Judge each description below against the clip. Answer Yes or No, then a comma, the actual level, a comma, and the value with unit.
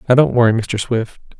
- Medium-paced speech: No, fast, 215 wpm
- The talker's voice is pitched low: Yes, low, 120 Hz